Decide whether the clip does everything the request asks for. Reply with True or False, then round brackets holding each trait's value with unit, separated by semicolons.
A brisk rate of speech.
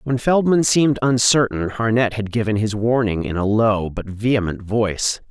False (170 wpm)